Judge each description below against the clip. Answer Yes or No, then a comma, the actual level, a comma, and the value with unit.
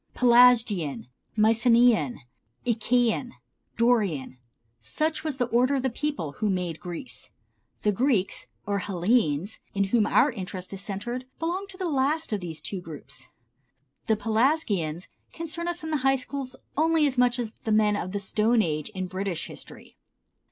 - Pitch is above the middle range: Yes, high, 225 Hz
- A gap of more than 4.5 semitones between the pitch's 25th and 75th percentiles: Yes, wide, 5.6 semitones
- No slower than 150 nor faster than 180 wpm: Yes, average, 155 wpm